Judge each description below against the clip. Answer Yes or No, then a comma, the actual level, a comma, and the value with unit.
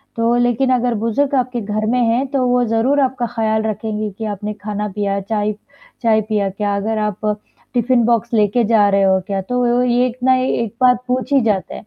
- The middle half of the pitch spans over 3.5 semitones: No, average, 2.8 semitones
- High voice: Yes, high, 225 Hz